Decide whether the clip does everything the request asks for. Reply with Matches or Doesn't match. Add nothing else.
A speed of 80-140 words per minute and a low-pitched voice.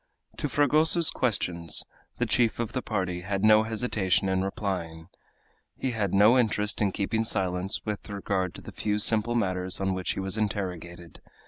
Doesn't match